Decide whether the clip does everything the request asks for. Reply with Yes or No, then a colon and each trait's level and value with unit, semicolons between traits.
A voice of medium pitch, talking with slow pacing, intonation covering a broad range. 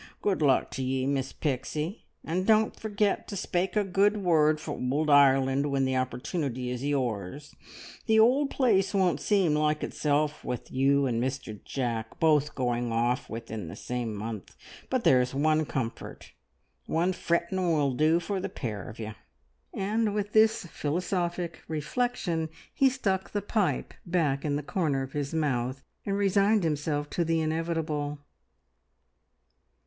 No: medium, 150 Hz; average, 155 wpm; wide, 6.0 semitones